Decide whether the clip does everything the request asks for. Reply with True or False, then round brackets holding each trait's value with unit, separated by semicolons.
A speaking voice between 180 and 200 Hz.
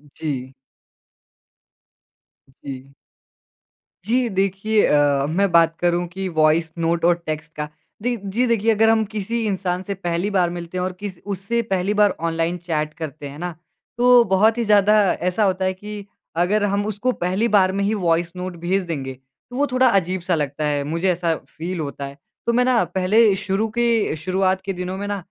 True (185 Hz)